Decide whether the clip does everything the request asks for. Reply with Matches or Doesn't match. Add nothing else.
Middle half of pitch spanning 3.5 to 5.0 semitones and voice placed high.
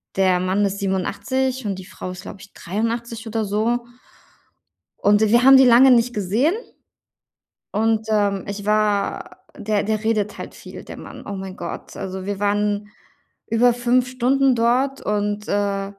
Doesn't match